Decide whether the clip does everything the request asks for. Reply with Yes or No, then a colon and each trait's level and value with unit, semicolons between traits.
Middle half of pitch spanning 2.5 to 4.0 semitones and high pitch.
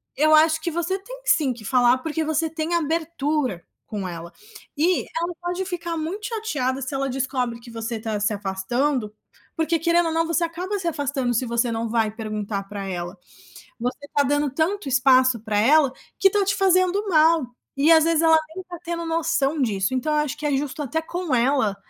No: wide, 5.6 semitones; very high, 295 Hz